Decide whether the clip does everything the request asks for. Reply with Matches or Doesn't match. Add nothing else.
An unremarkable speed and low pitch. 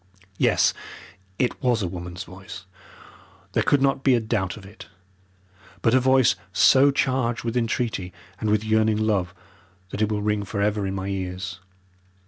Matches